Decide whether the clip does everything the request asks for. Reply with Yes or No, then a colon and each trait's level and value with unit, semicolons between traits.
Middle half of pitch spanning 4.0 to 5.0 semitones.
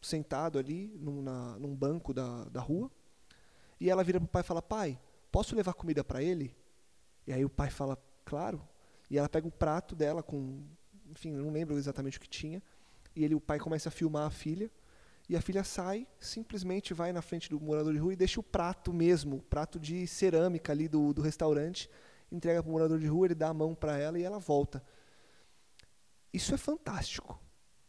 No: average, 3.4 semitones